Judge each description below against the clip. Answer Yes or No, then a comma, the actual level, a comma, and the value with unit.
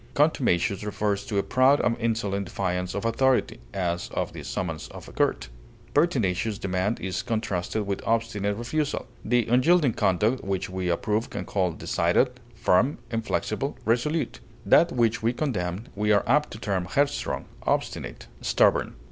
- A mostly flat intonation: No, average, 4.5 semitones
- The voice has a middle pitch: No, low, 105 Hz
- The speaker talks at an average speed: Yes, average, 150 wpm